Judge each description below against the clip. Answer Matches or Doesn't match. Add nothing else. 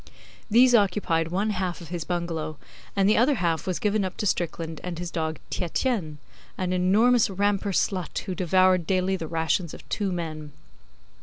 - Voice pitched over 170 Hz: Matches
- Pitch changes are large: Doesn't match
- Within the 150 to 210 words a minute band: Matches